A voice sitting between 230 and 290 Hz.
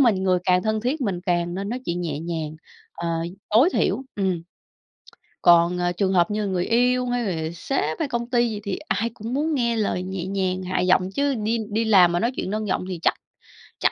No: high, 195 Hz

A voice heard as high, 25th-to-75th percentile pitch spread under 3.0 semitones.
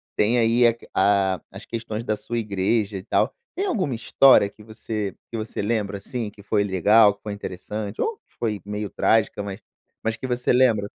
No: low, 110 Hz; narrow, 2.4 semitones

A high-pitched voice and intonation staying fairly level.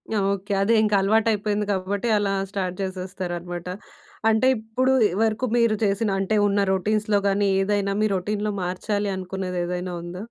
Yes: high, 200 Hz; narrow, 2.3 semitones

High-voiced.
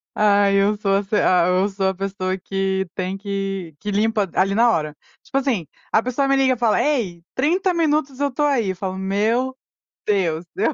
Yes: high, 200 Hz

